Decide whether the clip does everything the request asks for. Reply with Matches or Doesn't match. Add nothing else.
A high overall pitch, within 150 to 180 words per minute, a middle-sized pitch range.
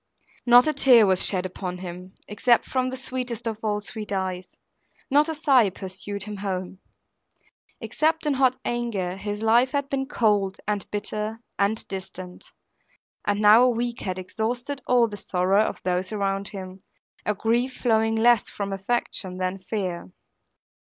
Matches